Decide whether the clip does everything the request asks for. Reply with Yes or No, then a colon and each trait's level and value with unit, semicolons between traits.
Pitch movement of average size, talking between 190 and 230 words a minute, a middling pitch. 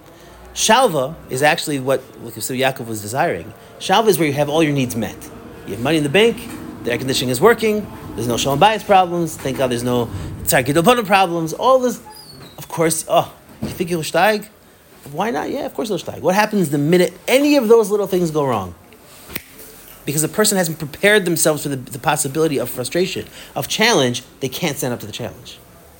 No: wide, 6.6 semitones; average, 200 wpm; medium, 155 Hz